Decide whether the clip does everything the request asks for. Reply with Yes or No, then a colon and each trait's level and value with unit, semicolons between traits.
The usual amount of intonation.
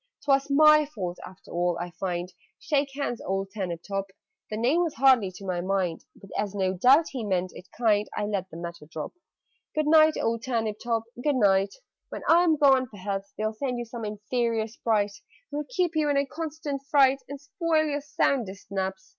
No: wide, 6.7 semitones